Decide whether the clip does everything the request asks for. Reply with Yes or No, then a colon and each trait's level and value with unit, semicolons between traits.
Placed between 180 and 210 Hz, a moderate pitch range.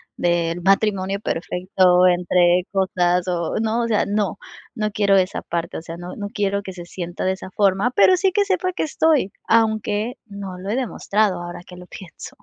Yes: high, 195 Hz; average, 3.2 semitones